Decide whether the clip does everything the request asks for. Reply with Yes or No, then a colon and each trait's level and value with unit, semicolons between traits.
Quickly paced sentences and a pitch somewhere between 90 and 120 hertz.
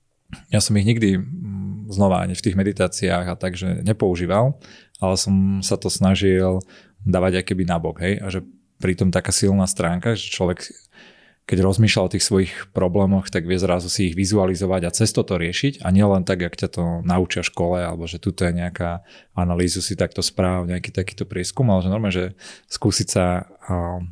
Yes: fast, 180 wpm; very low, 95 Hz